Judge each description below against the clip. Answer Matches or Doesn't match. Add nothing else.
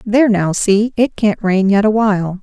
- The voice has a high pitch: Matches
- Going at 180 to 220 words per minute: Matches